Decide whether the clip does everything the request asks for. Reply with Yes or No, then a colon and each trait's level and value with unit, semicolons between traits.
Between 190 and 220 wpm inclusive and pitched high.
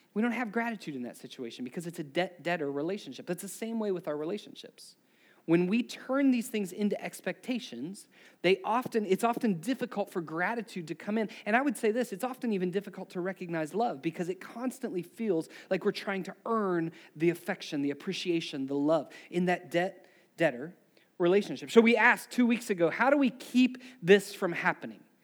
Yes: average, 195 wpm; high, 195 Hz